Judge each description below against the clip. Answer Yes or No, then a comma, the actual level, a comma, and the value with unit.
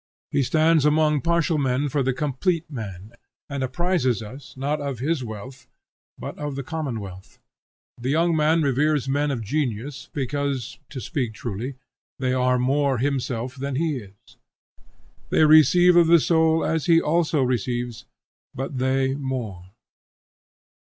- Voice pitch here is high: No, low, 135 Hz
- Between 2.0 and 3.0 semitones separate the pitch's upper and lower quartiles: No, average, 3.5 semitones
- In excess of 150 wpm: No, average, 145 wpm